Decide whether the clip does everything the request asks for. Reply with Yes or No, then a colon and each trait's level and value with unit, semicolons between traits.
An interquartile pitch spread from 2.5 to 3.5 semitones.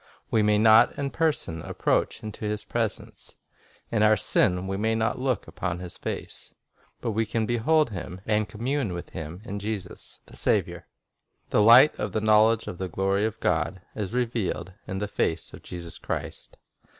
Yes: average, 3.0 semitones